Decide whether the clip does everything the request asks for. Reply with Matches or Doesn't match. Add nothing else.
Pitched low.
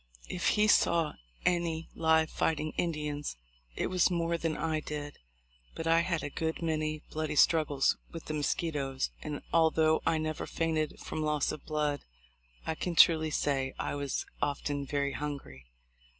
Doesn't match